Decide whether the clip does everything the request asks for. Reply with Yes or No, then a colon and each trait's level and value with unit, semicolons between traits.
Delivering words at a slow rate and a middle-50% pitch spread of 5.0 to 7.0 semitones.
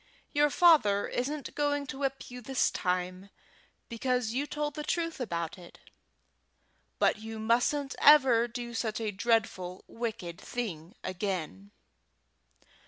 Yes: slow, 125 wpm; wide, 5.5 semitones